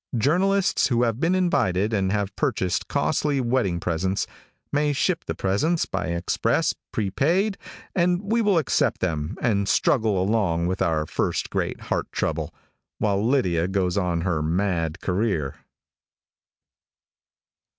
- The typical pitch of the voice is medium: No, low, 100 Hz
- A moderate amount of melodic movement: No, wide, 8.0 semitones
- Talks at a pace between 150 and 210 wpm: No, slow, 135 wpm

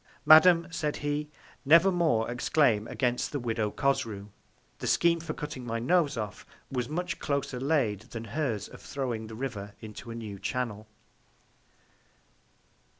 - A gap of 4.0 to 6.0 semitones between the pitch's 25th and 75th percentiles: Yes, average, 5.3 semitones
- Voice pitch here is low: Yes, low, 125 Hz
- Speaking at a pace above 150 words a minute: No, average, 145 wpm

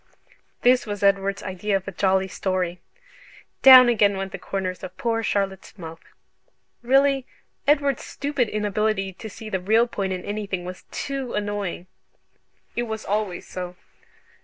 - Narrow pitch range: No, average, 3.4 semitones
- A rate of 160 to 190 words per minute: No, average, 145 wpm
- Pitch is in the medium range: No, high, 205 Hz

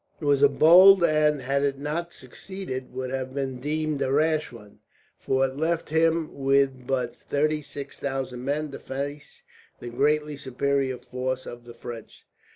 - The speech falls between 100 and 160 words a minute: No, average, 170 wpm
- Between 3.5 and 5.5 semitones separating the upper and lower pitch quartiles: No, average, 2.8 semitones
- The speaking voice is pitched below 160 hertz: Yes, medium, 140 Hz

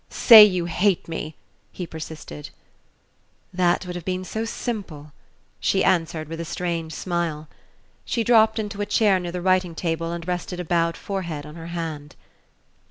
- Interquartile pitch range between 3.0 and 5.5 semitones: No, narrow, 2.5 semitones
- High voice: No, medium, 175 Hz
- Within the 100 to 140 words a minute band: No, average, 165 wpm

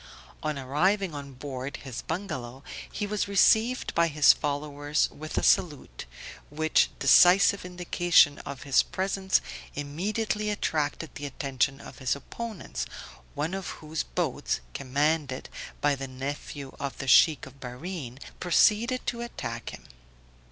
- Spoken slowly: Yes, slow, 130 wpm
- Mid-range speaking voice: Yes, medium, 150 Hz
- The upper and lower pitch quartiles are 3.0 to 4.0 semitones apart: No, average, 5.3 semitones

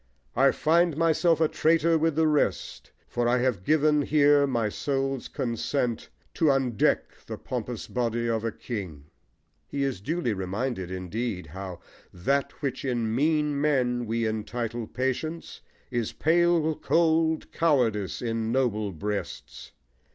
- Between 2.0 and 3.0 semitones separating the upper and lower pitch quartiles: No, average, 5.3 semitones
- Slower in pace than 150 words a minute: Yes, slow, 135 wpm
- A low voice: Yes, low, 130 Hz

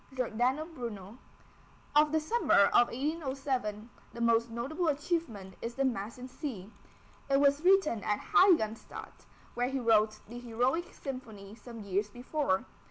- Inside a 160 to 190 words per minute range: No, average, 140 wpm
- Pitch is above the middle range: Yes, high, 245 Hz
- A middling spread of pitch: Yes, average, 4.8 semitones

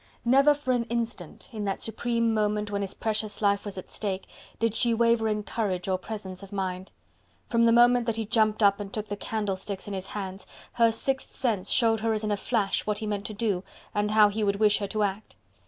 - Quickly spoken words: Yes, fast, 230 wpm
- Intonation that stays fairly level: Yes, narrow, 2.3 semitones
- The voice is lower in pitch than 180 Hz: No, high, 210 Hz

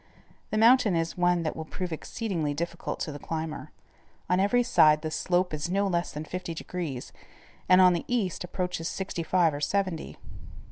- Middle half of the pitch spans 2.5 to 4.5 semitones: Yes, average, 2.8 semitones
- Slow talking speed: No, average, 180 wpm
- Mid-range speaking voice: Yes, medium, 175 Hz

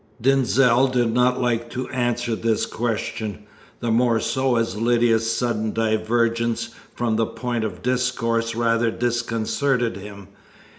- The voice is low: Yes, low, 115 Hz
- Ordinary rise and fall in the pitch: No, narrow, 1.5 semitones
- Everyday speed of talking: No, slow, 130 wpm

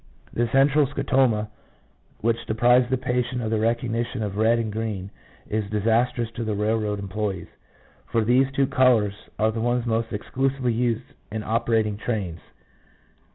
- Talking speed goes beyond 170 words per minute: No, average, 155 wpm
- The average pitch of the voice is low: Yes, low, 115 Hz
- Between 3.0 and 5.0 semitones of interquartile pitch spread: No, narrow, 2.4 semitones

